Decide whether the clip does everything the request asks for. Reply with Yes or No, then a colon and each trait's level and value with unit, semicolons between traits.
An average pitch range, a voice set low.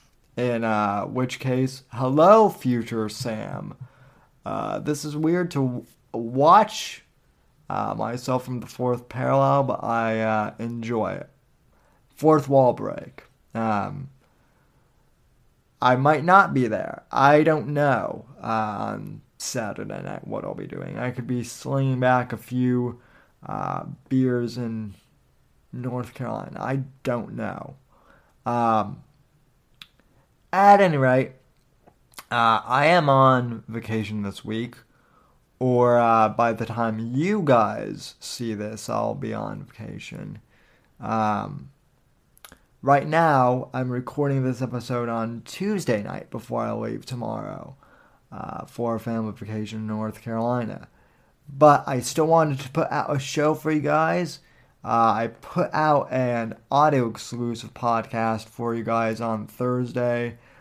Yes: average, 3.4 semitones; low, 125 Hz